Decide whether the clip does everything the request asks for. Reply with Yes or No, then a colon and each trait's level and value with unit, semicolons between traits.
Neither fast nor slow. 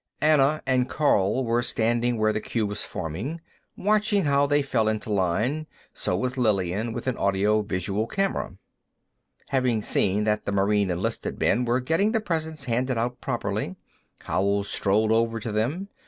Yes: average, 155 wpm